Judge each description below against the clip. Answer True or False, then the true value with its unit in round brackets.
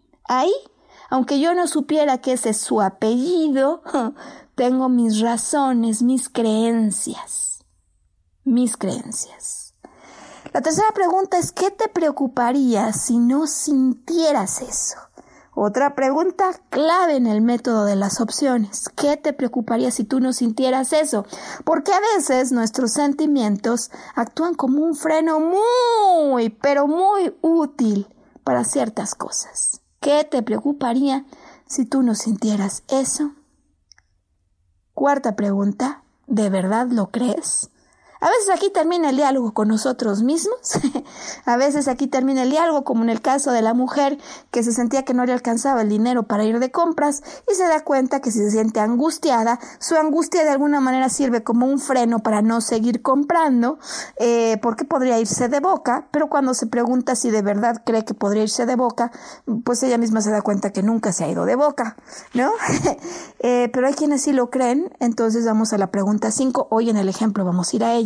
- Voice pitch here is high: True (255 Hz)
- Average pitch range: True (4.4 semitones)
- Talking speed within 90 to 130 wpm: False (165 wpm)